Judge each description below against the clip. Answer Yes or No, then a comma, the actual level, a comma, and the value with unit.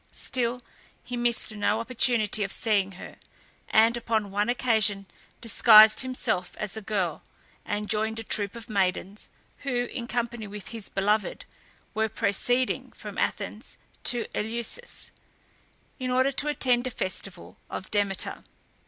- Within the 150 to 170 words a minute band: No, slow, 135 wpm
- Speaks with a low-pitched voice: No, high, 220 Hz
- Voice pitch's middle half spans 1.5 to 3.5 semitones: Yes, average, 2.8 semitones